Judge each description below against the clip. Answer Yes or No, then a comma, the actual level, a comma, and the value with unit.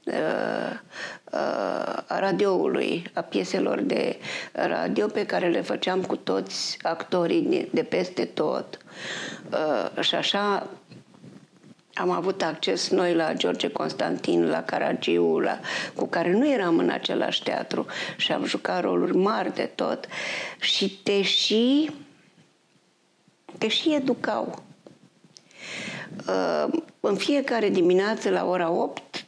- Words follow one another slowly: Yes, slow, 110 wpm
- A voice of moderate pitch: No, high, 200 Hz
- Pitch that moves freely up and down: Yes, wide, 7.8 semitones